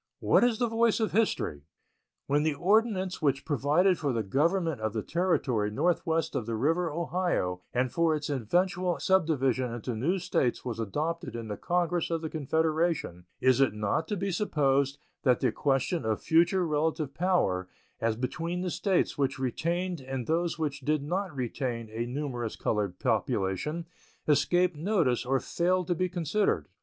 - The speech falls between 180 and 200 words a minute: No, average, 165 wpm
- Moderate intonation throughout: No, wide, 5.8 semitones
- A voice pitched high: No, medium, 155 Hz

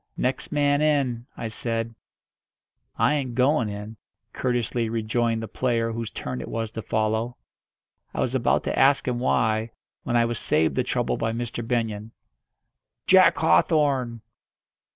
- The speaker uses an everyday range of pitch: No, narrow, 2.3 semitones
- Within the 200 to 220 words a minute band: No, average, 150 wpm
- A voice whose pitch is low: Yes, low, 115 Hz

